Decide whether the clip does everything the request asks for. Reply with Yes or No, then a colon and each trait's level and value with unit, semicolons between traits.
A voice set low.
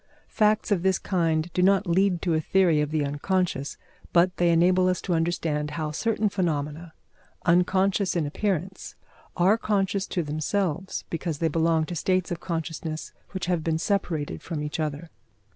No: medium, 175 Hz